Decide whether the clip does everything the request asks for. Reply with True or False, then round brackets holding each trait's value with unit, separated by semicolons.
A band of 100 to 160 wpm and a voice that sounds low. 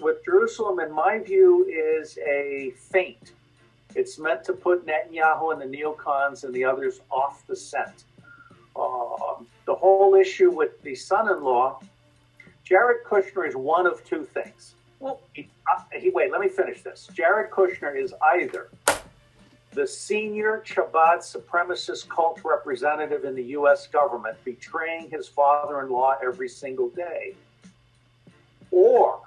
False (135 wpm; 190 Hz)